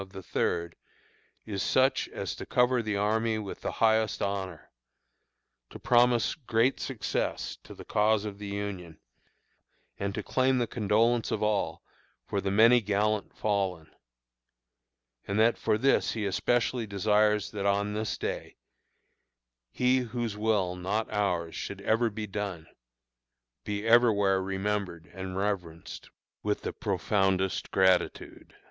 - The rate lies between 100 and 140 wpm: Yes, slow, 135 wpm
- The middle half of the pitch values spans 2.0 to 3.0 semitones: Yes, narrow, 2.5 semitones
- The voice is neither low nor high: No, low, 105 Hz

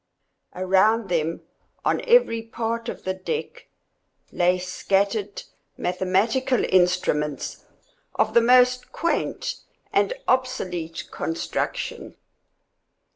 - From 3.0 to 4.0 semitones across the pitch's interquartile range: No, average, 4.7 semitones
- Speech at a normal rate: No, slow, 85 wpm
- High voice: Yes, high, 195 Hz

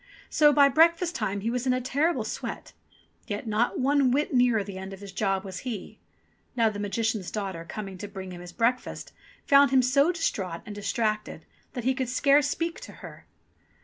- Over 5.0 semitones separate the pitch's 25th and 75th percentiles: Yes, wide, 5.4 semitones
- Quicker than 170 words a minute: Yes, average, 195 wpm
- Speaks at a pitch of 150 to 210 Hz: No, high, 230 Hz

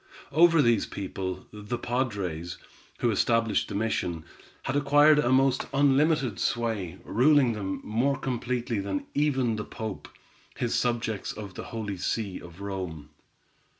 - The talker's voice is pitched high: No, low, 115 Hz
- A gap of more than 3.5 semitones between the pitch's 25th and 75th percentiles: Yes, average, 5.2 semitones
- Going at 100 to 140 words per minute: Yes, slow, 135 wpm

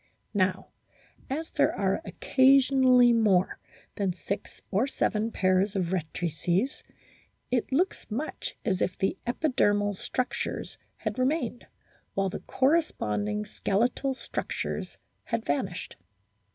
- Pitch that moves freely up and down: Yes, wide, 5.8 semitones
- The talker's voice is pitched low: No, high, 215 Hz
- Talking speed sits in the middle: No, slow, 110 wpm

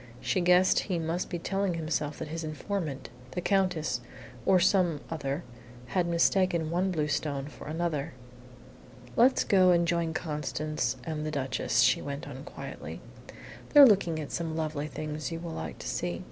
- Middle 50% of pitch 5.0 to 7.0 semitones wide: No, average, 3.0 semitones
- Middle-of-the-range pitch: Yes, medium, 165 Hz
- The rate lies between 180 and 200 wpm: No, average, 165 wpm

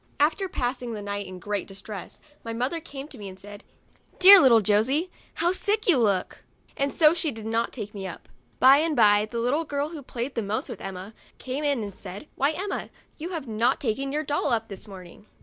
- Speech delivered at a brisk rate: Yes, fast, 230 wpm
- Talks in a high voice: Yes, high, 245 Hz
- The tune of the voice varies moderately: No, wide, 6.2 semitones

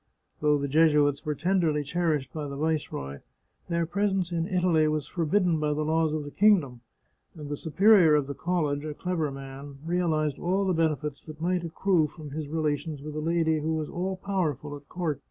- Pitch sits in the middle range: Yes, medium, 155 Hz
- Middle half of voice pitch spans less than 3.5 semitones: Yes, average, 2.9 semitones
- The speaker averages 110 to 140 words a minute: No, average, 190 wpm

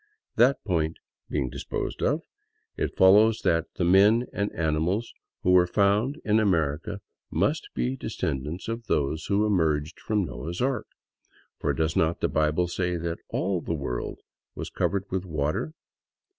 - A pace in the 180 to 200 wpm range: No, average, 155 wpm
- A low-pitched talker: Yes, very low, 90 Hz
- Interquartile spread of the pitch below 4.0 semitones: No, average, 4.7 semitones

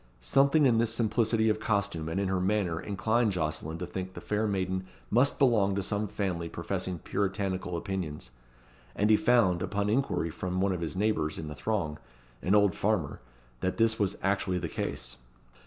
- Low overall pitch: Yes, low, 100 Hz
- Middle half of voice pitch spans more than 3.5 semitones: No, average, 3.1 semitones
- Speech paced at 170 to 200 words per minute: Yes, average, 180 wpm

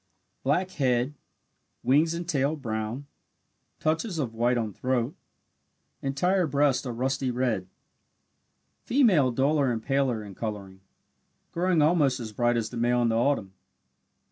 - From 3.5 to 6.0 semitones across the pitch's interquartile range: Yes, average, 4.2 semitones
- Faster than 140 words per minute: No, slow, 135 wpm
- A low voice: Yes, low, 130 Hz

